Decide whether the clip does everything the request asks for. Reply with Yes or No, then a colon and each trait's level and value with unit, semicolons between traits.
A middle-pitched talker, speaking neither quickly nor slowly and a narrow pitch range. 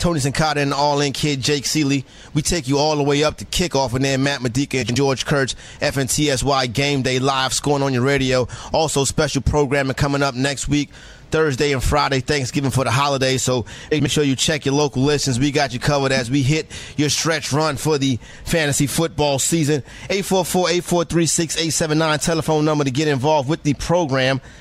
Yes: medium, 145 Hz; average, 195 wpm; narrow, 2.3 semitones